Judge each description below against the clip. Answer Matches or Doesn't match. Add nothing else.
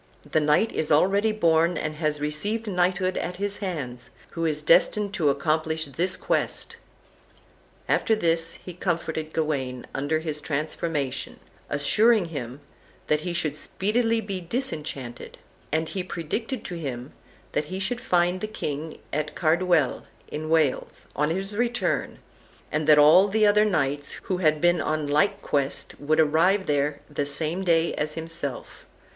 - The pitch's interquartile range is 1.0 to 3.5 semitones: Doesn't match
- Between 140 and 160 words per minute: Matches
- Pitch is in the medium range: Matches